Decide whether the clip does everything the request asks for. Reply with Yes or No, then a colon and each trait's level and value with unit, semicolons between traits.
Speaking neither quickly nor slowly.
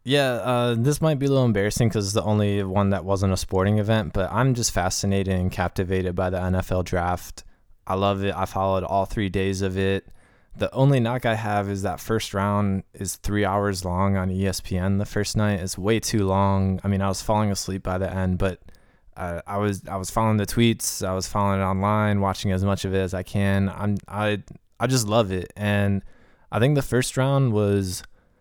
No: fast, 220 wpm